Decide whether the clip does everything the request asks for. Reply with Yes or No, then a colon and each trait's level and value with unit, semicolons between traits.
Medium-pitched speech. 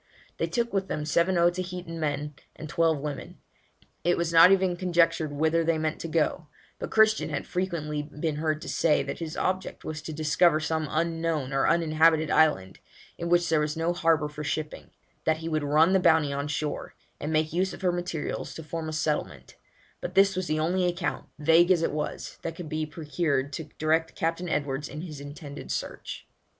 Yes: medium, 160 Hz